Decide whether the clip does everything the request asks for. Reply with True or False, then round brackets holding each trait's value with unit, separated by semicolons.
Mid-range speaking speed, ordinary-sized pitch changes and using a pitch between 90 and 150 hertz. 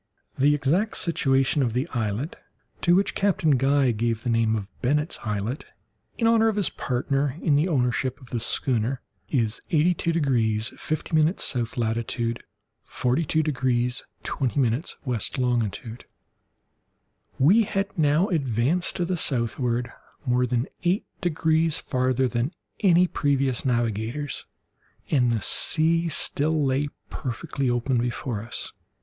False (130 wpm; 4.8 semitones; 135 Hz)